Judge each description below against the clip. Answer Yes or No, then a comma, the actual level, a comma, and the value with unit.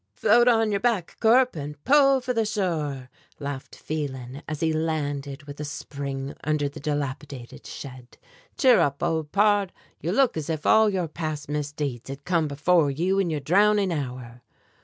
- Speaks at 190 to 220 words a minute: No, average, 170 wpm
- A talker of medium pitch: Yes, medium, 155 Hz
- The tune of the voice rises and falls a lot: Yes, wide, 5.7 semitones